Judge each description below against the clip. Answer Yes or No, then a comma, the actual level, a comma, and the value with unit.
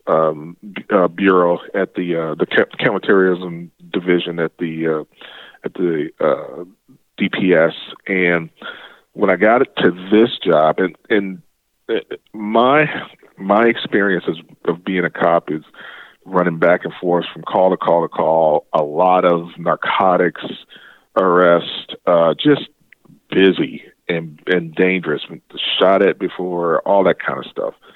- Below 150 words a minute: Yes, average, 140 wpm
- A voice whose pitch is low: Yes, very low, 90 Hz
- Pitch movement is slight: Yes, narrow, 2.3 semitones